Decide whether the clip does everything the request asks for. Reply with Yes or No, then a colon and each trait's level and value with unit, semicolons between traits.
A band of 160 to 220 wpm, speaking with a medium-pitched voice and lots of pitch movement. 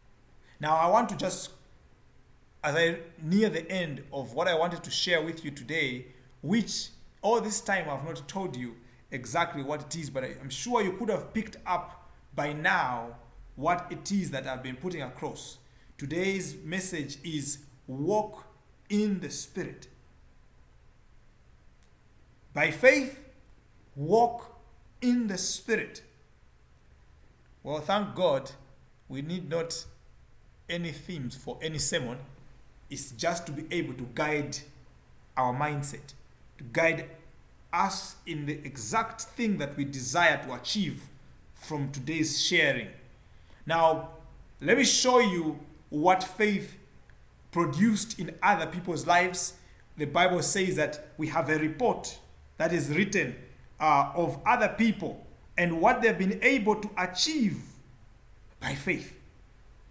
No: slow, 135 wpm; medium, 160 Hz; wide, 6.1 semitones